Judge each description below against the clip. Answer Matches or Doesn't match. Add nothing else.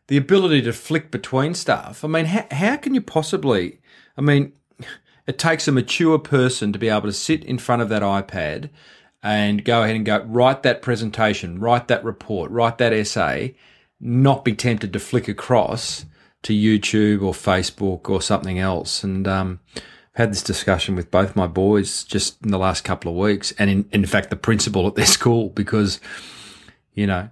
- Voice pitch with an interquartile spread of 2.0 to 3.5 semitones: Doesn't match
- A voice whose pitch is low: Matches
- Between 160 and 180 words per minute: Doesn't match